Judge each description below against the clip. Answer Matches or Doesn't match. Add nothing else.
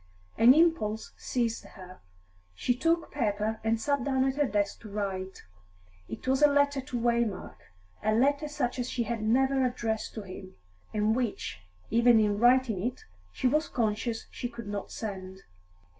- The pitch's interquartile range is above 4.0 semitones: Doesn't match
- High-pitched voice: Matches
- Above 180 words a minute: Doesn't match